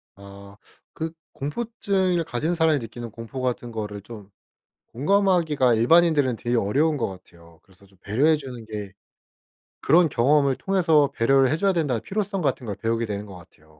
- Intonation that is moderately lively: No, wide, 7.0 semitones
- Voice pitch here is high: No, low, 130 Hz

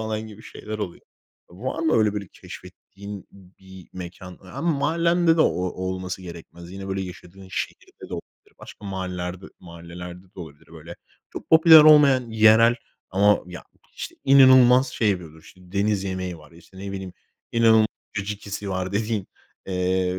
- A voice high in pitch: No, very low, 95 Hz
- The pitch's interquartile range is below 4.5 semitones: Yes, average, 3.4 semitones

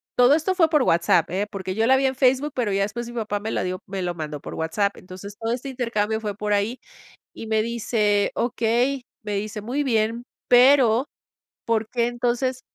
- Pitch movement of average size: Yes, average, 3.4 semitones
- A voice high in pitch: Yes, high, 225 Hz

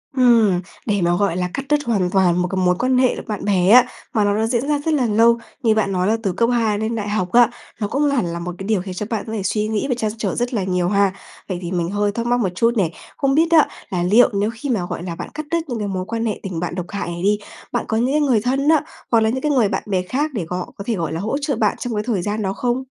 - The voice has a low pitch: No, high, 215 Hz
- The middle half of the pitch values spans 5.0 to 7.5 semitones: No, average, 4.5 semitones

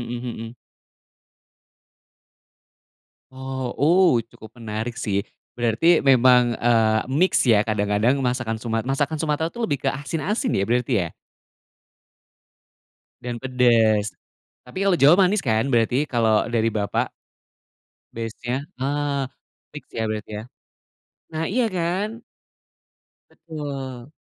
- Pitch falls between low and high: No, low, 125 Hz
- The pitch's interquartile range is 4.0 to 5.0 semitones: Yes, average, 4.5 semitones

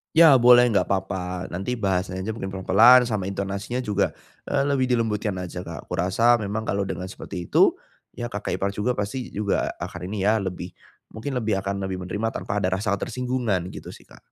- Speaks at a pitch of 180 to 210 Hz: No, low, 100 Hz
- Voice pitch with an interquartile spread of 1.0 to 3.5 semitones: No, average, 3.9 semitones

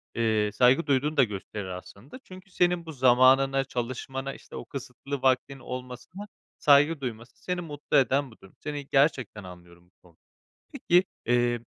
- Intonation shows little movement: No, average, 3.6 semitones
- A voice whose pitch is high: No, low, 130 Hz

